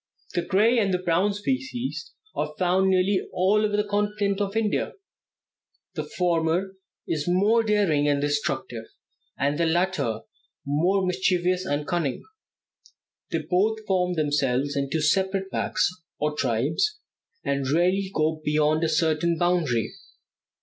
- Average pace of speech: No, slow, 130 wpm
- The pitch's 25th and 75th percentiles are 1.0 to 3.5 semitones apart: No, average, 4.7 semitones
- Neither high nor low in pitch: Yes, medium, 175 Hz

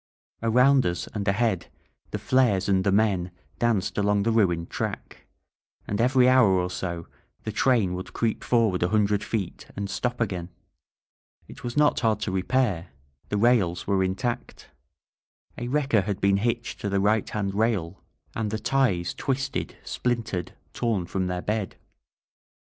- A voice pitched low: Yes, low, 105 Hz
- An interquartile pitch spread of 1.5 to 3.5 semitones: No, average, 4.0 semitones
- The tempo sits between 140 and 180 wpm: Yes, average, 160 wpm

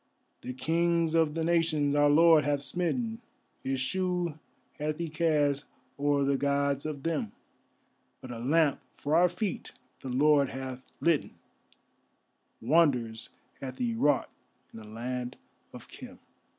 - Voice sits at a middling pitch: Yes, medium, 145 Hz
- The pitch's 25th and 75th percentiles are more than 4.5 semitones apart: No, average, 3.7 semitones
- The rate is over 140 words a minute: No, slow, 135 wpm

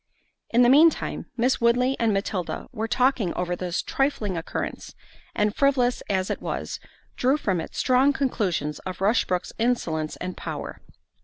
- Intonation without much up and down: No, wide, 5.6 semitones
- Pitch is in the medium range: No, high, 225 Hz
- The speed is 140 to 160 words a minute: Yes, average, 155 wpm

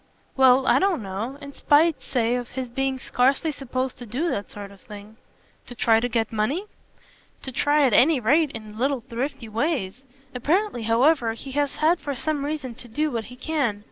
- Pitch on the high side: Yes, very high, 255 Hz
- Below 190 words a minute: No, average, 195 wpm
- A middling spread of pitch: Yes, average, 4.2 semitones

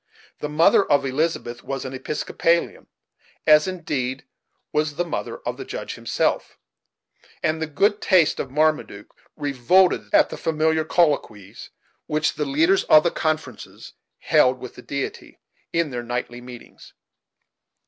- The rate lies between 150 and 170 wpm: No, average, 140 wpm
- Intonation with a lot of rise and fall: No, average, 4.3 semitones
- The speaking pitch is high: No, medium, 150 Hz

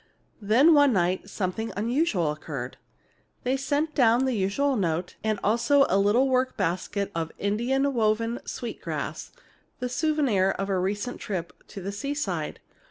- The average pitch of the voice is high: Yes, high, 220 Hz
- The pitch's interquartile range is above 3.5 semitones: Yes, wide, 5.4 semitones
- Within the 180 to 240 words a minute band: No, average, 155 wpm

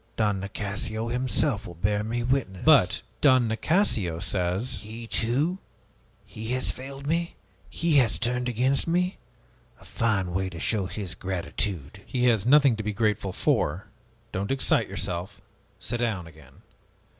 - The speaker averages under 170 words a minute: Yes, average, 150 wpm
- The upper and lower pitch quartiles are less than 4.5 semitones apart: No, average, 4.8 semitones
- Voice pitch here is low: Yes, low, 110 Hz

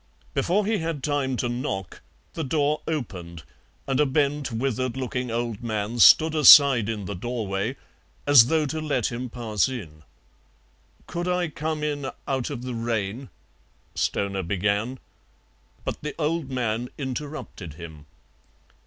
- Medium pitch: No, low, 125 Hz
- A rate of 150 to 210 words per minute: No, average, 140 wpm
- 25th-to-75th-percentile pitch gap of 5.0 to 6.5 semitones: Yes, average, 5.3 semitones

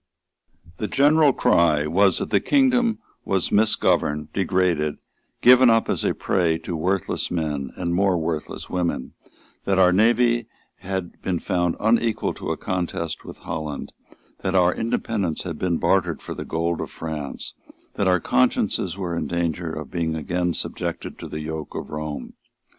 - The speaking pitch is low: Yes, very low, 90 Hz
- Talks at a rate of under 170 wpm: Yes, average, 160 wpm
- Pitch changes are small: No, average, 3.7 semitones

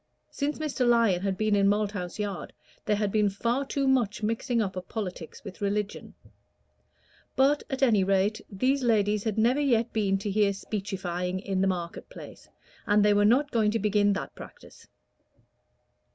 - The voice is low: No, high, 210 Hz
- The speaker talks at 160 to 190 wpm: Yes, average, 170 wpm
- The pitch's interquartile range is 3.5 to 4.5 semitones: No, average, 2.9 semitones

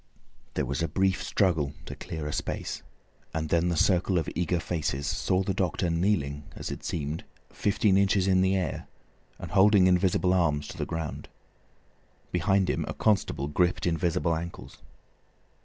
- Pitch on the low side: Yes, very low, 90 Hz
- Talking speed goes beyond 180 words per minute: No, average, 160 wpm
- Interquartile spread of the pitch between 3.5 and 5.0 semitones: No, average, 3.1 semitones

